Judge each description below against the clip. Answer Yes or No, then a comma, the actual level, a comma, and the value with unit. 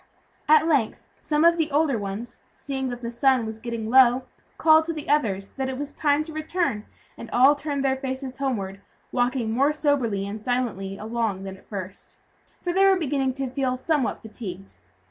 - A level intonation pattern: No, average, 4.7 semitones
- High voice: Yes, very high, 260 Hz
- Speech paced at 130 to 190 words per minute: Yes, average, 185 wpm